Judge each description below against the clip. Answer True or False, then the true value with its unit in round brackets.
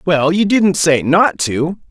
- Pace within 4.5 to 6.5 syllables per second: False (3.5 syllables/s)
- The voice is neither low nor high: True (170 Hz)